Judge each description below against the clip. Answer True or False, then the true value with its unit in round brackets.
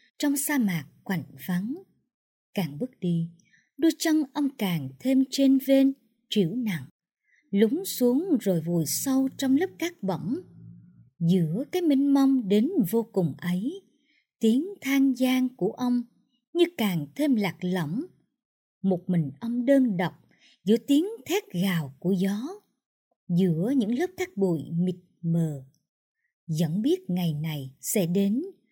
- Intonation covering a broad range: True (7.4 semitones)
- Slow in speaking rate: True (140 wpm)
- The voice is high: True (225 Hz)